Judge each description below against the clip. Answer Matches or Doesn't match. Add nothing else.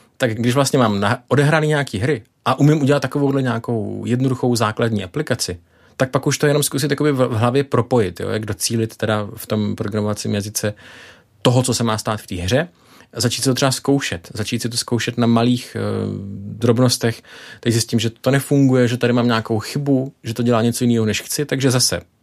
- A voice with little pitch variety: Doesn't match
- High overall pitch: Doesn't match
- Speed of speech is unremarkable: Doesn't match